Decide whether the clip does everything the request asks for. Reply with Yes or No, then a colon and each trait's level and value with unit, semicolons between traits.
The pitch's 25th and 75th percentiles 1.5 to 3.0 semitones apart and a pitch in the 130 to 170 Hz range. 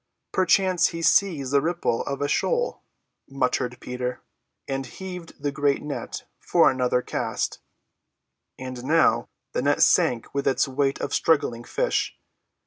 No: average, 4.7 semitones; medium, 140 Hz